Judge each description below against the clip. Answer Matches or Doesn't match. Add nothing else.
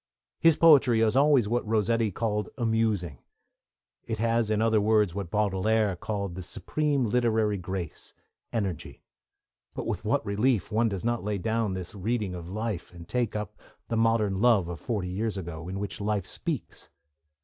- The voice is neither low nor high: Doesn't match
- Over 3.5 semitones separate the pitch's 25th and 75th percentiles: Doesn't match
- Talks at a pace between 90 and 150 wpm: Doesn't match